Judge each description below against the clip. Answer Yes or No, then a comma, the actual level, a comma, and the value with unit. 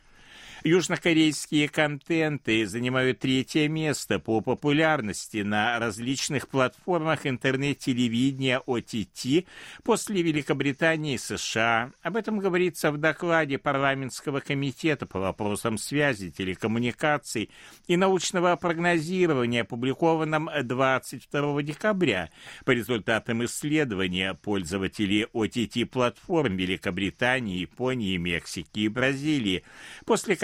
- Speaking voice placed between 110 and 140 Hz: Yes, low, 135 Hz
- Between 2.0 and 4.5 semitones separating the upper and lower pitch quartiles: No, wide, 5.4 semitones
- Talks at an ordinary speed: No, slow, 85 wpm